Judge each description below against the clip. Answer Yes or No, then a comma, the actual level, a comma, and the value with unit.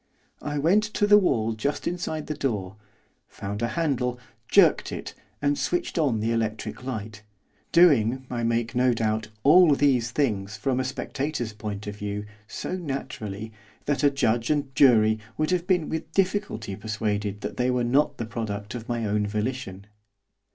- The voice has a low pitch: Yes, low, 120 Hz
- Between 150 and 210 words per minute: Yes, average, 165 wpm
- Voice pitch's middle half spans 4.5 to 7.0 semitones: Yes, average, 5.2 semitones